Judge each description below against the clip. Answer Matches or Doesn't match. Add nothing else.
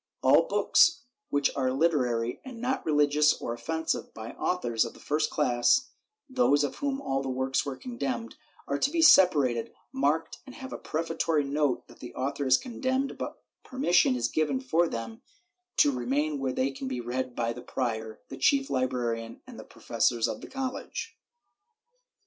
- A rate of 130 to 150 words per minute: Doesn't match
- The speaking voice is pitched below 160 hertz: Matches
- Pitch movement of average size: Doesn't match